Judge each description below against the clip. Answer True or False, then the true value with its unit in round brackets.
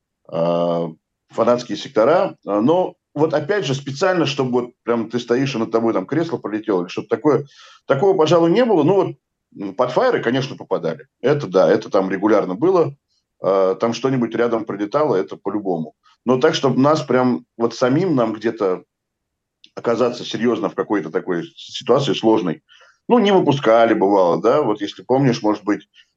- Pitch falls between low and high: False (120 Hz)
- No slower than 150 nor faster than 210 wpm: True (155 wpm)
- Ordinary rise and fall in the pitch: True (4.7 semitones)